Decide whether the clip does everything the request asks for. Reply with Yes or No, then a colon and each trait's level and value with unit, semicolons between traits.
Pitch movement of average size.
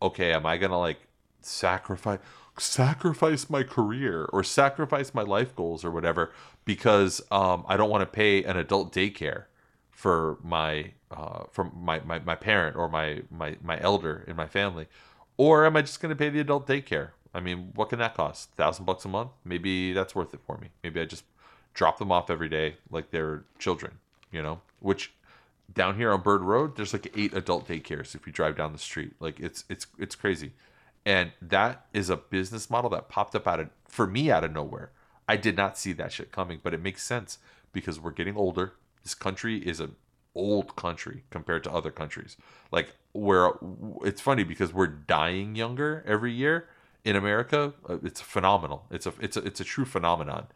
No: wide, 5.9 semitones